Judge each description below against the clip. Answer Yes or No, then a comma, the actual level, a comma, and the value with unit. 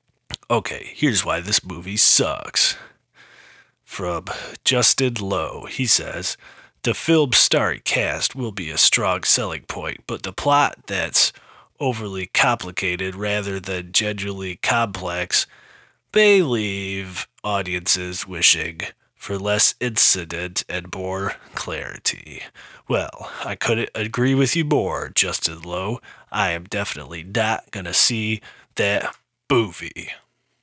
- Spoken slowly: Yes, slow, 115 wpm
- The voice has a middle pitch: No, low, 100 Hz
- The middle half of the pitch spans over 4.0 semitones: Yes, average, 4.5 semitones